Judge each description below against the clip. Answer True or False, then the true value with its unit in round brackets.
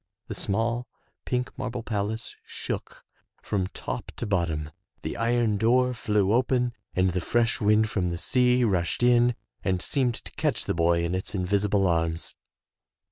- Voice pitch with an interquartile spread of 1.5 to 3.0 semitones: False (4.7 semitones)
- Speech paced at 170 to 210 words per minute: False (155 wpm)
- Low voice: True (105 Hz)